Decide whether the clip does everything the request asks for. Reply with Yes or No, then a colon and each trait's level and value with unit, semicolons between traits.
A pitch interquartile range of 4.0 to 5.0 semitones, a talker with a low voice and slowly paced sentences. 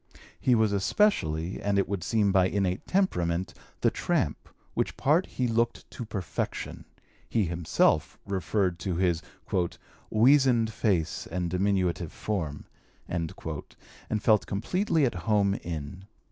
Yes: average, 4.4 semitones; low, 100 Hz; slow, 125 wpm